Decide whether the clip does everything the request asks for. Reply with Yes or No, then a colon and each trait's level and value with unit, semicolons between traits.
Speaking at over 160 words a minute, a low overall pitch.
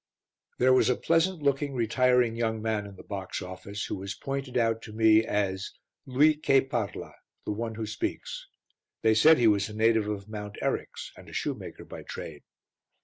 Yes: average, 185 wpm; low, 115 Hz